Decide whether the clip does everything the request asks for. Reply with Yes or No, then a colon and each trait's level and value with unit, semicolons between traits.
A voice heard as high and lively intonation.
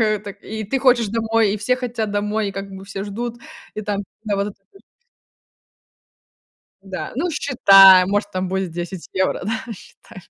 No: high, 205 Hz; narrow, 2.5 semitones